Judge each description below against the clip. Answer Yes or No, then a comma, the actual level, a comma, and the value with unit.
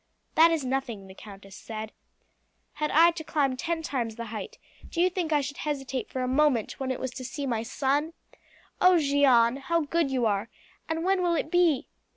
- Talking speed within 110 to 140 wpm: No, average, 200 wpm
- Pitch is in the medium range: No, very high, 275 Hz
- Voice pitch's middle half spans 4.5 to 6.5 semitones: Yes, average, 5.0 semitones